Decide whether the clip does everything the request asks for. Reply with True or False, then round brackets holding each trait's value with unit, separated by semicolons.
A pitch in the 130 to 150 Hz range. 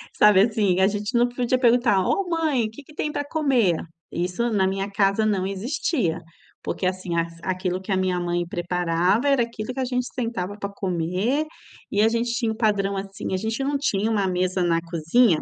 False (205 Hz)